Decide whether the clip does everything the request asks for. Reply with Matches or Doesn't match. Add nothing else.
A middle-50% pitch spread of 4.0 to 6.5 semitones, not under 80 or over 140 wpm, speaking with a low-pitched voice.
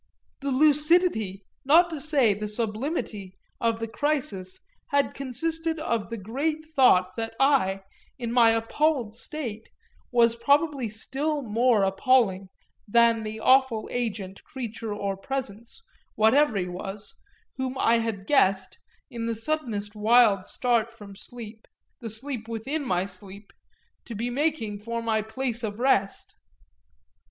Doesn't match